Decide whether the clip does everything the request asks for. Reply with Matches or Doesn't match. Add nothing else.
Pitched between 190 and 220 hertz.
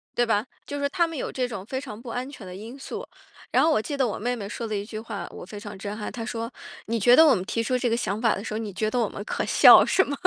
Doesn't match